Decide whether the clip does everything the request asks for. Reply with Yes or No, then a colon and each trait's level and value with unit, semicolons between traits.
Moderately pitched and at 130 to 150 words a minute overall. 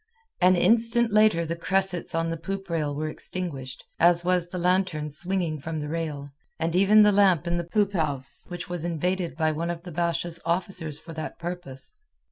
No: medium, 170 Hz; average, 190 wpm